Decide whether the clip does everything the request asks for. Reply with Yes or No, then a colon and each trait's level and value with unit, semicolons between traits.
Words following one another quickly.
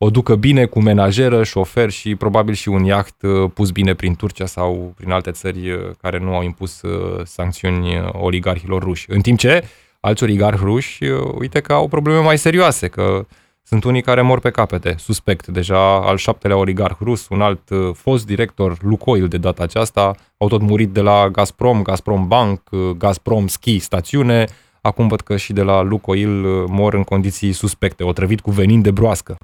Yes: fast, 175 wpm